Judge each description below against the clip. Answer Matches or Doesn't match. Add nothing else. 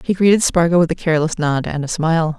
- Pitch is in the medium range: Matches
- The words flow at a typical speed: Doesn't match